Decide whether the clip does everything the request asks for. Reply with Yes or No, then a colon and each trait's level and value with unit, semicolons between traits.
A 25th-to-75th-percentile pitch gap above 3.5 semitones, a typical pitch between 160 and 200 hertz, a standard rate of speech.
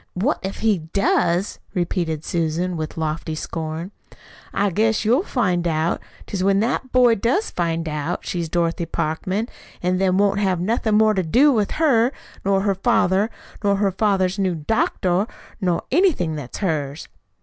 Yes: average, 4.1 semitones; medium, 185 Hz; average, 160 wpm